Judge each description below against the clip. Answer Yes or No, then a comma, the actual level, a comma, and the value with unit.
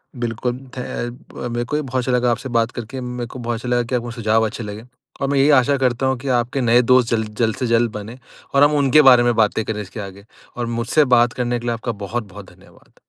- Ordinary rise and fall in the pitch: No, narrow, 1.8 semitones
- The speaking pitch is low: Yes, low, 120 Hz